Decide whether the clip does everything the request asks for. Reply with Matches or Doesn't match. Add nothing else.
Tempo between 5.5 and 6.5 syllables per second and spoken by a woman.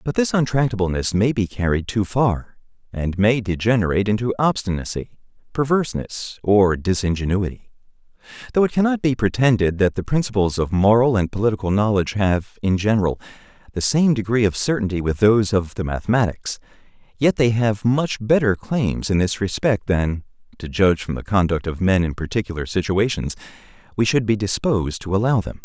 Doesn't match